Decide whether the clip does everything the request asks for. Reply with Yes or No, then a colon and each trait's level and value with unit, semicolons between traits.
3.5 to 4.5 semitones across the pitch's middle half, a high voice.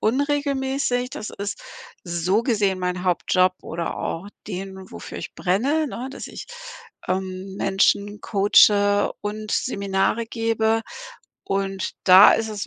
No: average, 3.0 semitones; high, 205 Hz